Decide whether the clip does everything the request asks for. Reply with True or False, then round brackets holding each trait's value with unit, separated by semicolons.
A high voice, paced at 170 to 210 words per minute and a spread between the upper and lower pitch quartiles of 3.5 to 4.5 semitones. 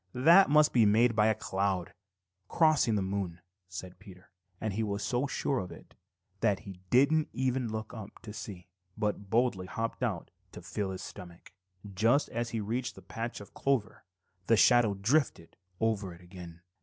False (110 Hz; 175 wpm; 4.0 semitones)